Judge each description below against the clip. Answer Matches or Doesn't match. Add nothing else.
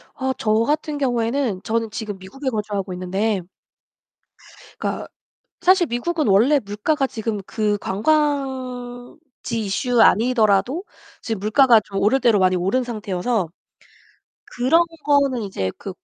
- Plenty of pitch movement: Doesn't match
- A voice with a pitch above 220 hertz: Matches